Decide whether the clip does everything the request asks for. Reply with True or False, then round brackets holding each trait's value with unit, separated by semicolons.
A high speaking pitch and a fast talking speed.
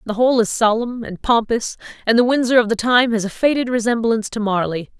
True (230 Hz; 215 wpm)